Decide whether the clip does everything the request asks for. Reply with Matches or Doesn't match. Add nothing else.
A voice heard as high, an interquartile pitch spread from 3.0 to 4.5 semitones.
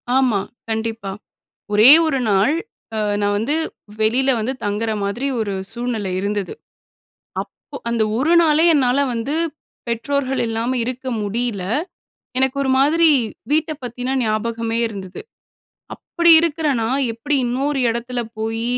Matches